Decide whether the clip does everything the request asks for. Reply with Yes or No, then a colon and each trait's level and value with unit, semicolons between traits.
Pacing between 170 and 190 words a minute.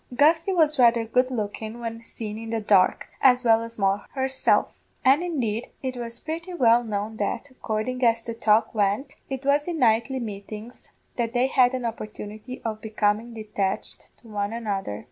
Yes: average, 175 wpm